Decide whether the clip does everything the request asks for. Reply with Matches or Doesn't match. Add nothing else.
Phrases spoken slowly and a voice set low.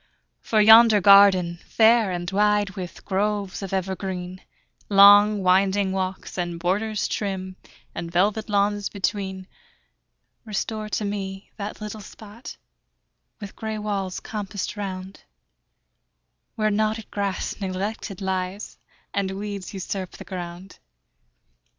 Doesn't match